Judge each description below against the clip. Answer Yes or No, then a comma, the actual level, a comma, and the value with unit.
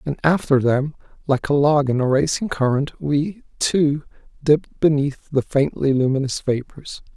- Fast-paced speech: No, average, 150 wpm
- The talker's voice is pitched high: No, medium, 140 Hz